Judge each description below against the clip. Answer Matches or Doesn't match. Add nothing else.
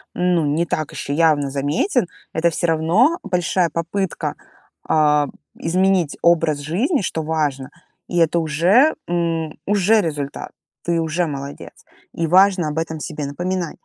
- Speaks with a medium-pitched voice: Matches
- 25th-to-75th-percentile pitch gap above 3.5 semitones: Doesn't match